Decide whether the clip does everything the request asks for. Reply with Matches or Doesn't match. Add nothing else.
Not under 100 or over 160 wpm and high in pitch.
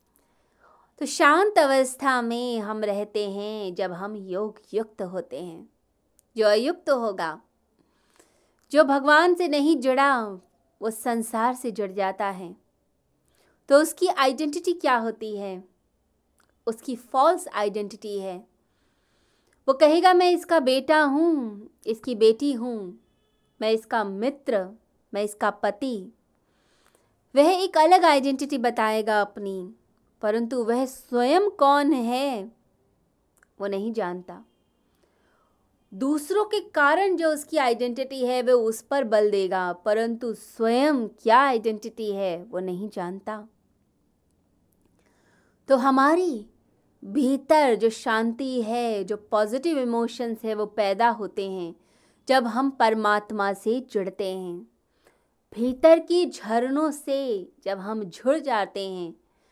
Matches